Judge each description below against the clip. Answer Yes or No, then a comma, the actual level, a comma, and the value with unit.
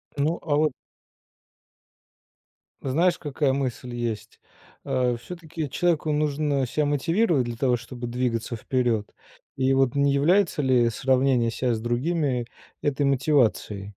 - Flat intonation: No, average, 3.6 semitones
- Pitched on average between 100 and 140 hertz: Yes, low, 135 Hz